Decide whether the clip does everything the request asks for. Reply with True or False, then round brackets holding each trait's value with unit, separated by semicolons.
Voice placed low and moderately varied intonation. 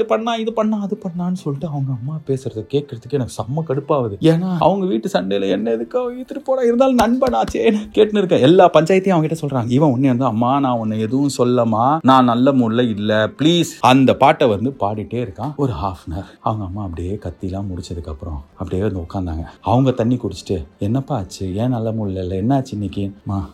False (125 Hz; 7.8 semitones)